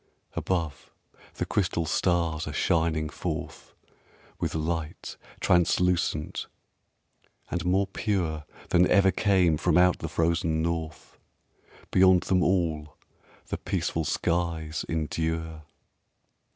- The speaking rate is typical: No, slow, 100 wpm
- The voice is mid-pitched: No, very low, 85 Hz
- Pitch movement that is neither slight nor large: No, narrow, 2.2 semitones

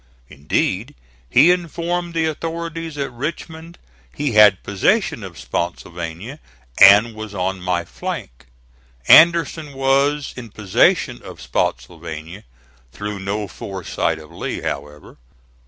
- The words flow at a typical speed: No, slow, 110 wpm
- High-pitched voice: No, low, 110 Hz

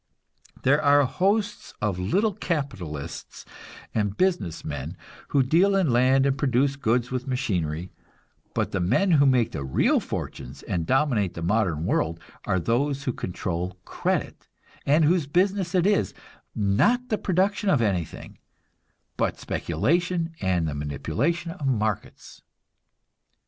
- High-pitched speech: No, low, 130 Hz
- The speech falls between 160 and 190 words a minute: No, slow, 135 wpm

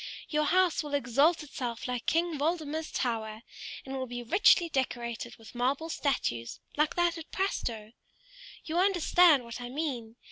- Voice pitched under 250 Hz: No, very high, 280 Hz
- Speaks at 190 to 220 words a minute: No, average, 150 wpm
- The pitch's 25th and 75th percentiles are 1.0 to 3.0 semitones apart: No, average, 5.3 semitones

